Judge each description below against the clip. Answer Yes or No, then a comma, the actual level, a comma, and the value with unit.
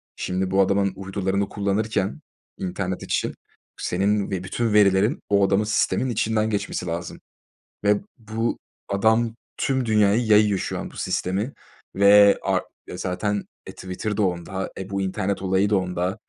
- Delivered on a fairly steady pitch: Yes, narrow, 1.9 semitones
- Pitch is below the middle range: Yes, low, 100 Hz